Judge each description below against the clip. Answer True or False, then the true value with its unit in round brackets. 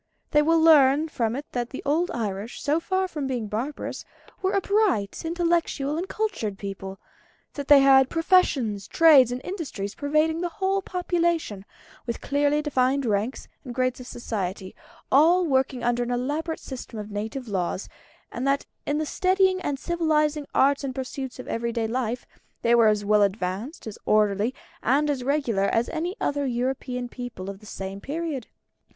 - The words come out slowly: False (170 wpm)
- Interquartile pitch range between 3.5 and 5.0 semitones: False (5.6 semitones)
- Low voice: False (265 Hz)